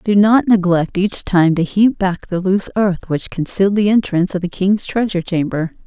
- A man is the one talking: No, female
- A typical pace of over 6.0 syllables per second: No, 5.2 syllables/s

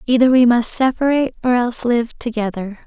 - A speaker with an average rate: Yes, average, 165 wpm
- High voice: Yes, high, 240 Hz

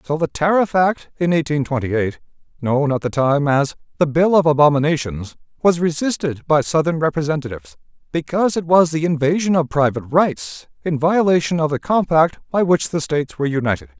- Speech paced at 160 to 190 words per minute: Yes, average, 175 wpm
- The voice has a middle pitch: Yes, medium, 155 Hz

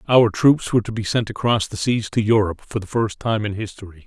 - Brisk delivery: Yes, fast, 250 wpm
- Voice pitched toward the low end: Yes, low, 105 Hz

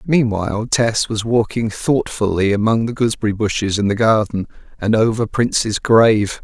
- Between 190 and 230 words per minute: No, average, 150 wpm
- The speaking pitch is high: No, low, 110 Hz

